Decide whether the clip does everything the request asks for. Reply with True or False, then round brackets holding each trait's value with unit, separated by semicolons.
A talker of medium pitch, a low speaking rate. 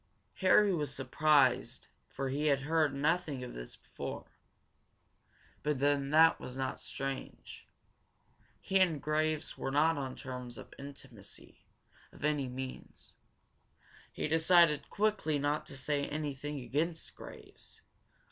True (145 Hz; 125 wpm)